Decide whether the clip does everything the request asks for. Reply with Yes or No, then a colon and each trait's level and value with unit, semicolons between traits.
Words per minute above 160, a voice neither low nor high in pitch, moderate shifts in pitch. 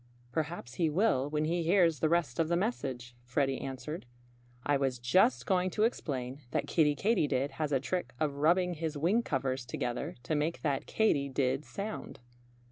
Yes: average, 175 wpm; medium, 150 Hz; average, 4.5 semitones